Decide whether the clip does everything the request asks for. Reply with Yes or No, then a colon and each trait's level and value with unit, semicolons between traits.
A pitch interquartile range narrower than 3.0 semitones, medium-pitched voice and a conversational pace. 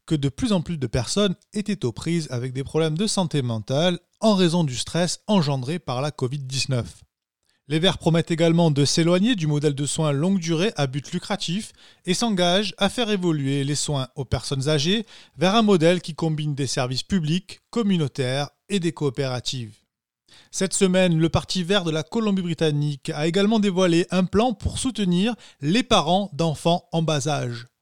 No: average, 5.1 semitones; medium, 165 Hz; average, 175 wpm